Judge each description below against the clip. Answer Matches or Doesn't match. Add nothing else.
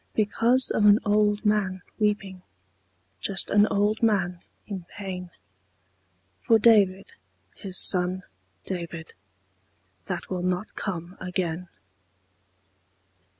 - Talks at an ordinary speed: Doesn't match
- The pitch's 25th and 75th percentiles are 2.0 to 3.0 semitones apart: Matches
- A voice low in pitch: Doesn't match